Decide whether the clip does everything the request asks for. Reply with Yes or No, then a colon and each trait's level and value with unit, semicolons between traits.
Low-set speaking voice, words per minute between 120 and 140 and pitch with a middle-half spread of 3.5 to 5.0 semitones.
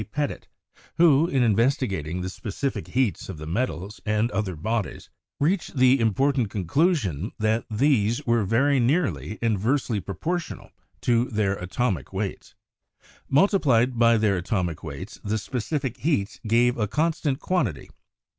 No: low, 115 Hz; slow, 135 wpm; wide, 5.4 semitones